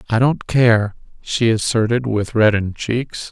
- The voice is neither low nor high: No, low, 115 Hz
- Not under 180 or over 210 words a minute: No, average, 145 wpm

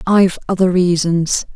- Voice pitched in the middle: Yes, medium, 180 Hz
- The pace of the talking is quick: No, slow, 115 wpm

